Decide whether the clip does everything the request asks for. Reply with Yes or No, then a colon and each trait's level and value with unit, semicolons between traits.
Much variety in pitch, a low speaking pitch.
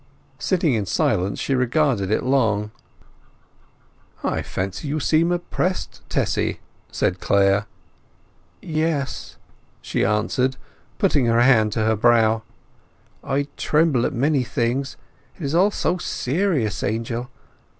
Yes: wide, 5.7 semitones; low, 125 Hz